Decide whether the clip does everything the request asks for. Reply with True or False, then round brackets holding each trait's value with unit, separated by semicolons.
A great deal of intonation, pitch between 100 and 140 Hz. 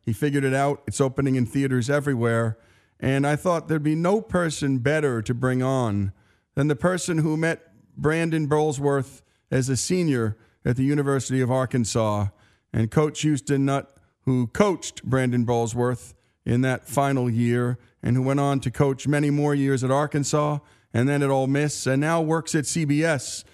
False (3.3 semitones; 135 Hz)